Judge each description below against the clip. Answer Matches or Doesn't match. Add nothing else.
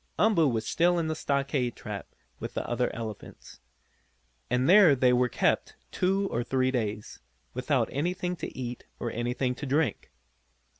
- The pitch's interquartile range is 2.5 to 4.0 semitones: Doesn't match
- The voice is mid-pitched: Doesn't match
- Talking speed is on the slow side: Doesn't match